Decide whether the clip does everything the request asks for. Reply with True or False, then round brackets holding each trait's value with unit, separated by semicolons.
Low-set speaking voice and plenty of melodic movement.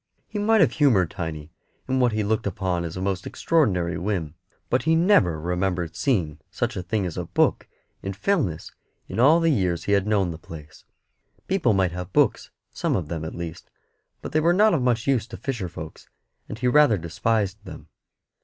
True (100 Hz; 6.9 semitones)